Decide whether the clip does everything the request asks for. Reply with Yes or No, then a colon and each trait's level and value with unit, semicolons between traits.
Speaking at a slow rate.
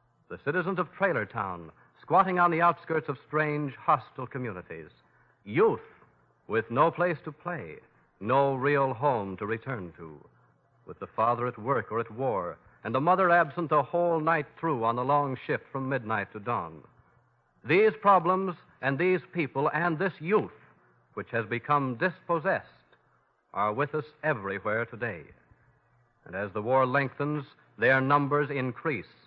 No: average, 150 wpm